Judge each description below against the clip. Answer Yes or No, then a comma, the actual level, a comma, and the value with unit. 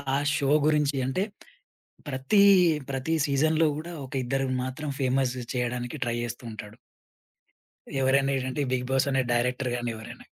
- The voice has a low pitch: Yes, low, 130 Hz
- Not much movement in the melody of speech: Yes, narrow, 2.2 semitones